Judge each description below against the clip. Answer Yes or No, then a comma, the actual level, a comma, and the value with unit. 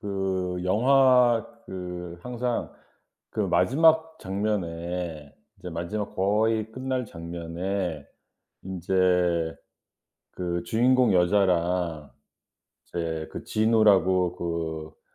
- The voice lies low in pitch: Yes, very low, 95 Hz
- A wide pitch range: No, average, 4.3 semitones